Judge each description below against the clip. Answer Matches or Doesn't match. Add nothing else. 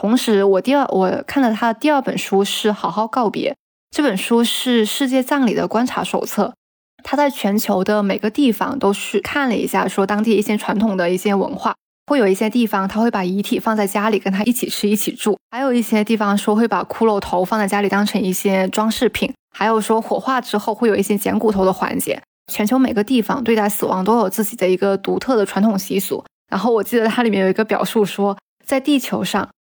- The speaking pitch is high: Matches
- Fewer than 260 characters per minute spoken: Doesn't match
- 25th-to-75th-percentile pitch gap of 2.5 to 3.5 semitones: Matches